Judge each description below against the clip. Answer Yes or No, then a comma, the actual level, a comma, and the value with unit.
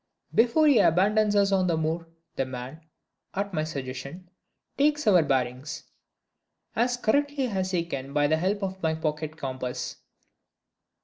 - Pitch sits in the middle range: Yes, medium, 170 Hz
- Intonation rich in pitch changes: Yes, wide, 5.9 semitones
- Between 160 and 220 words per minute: No, average, 145 wpm